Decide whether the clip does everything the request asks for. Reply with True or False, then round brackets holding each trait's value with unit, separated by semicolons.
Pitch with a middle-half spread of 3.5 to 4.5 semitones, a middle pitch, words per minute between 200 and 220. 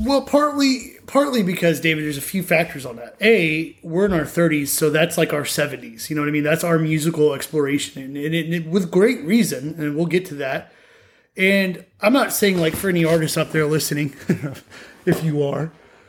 True (4.2 semitones; 165 Hz; 205 wpm)